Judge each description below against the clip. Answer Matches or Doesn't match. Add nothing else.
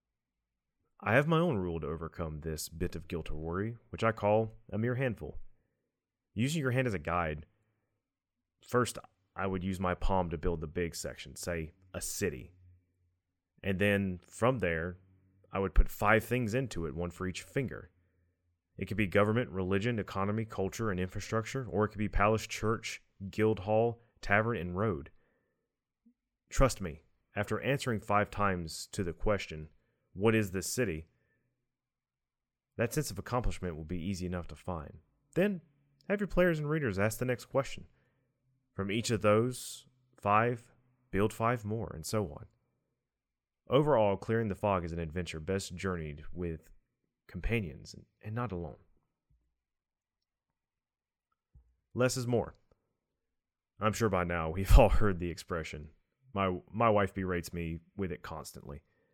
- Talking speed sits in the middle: Matches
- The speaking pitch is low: Matches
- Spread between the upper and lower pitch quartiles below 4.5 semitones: Doesn't match